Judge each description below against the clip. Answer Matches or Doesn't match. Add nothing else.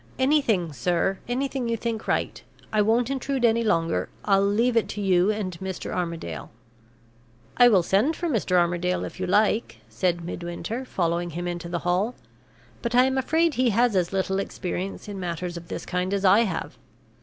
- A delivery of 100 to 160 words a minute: Doesn't match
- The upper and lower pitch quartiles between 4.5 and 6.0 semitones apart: Matches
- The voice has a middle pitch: Doesn't match